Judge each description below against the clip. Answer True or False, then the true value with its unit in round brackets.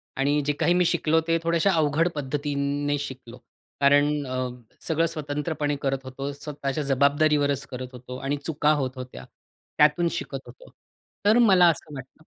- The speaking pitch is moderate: True (145 Hz)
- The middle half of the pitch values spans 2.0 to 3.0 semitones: True (2.5 semitones)